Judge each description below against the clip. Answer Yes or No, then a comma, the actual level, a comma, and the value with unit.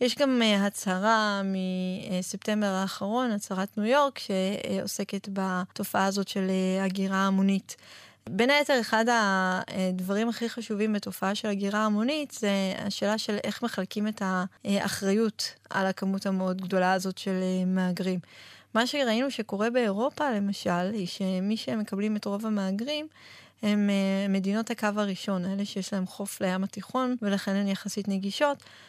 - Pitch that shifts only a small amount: Yes, narrow, 2.2 semitones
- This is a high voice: Yes, high, 200 Hz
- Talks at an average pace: Yes, average, 130 wpm